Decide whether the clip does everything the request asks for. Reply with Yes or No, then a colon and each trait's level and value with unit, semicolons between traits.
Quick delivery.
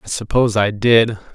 No: average, 180 wpm